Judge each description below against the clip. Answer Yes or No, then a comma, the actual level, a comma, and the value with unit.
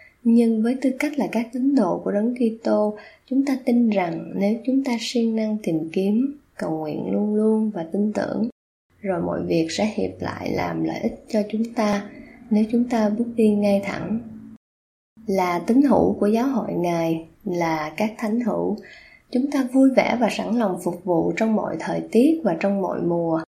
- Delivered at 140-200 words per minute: Yes, average, 195 wpm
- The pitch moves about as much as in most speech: Yes, average, 3.8 semitones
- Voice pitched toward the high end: Yes, high, 220 Hz